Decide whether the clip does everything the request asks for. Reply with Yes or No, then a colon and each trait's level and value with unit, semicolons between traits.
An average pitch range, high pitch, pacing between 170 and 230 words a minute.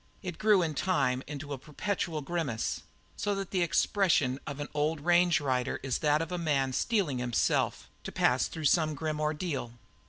No: average, 4.0 semitones; medium, 155 Hz; average, 180 wpm